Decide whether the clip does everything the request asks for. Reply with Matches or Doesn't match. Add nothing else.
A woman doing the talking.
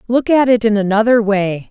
Matches